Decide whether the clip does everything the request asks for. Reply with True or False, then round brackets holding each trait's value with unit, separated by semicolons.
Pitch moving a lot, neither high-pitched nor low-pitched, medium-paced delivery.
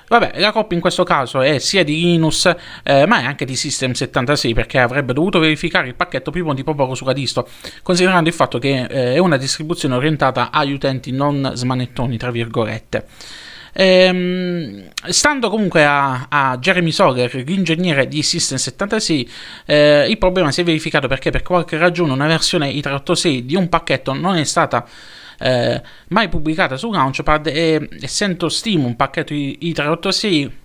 False (4.8 semitones; 155 Hz; 160 wpm)